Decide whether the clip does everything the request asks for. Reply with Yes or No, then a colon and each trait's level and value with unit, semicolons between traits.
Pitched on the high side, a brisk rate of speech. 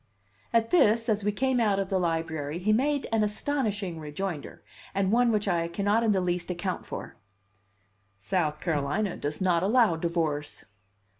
No: high, 195 Hz; average, 160 wpm